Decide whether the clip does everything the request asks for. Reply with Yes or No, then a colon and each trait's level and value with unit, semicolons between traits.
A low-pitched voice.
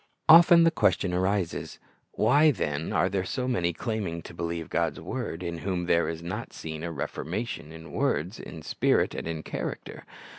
Yes: very low, 85 Hz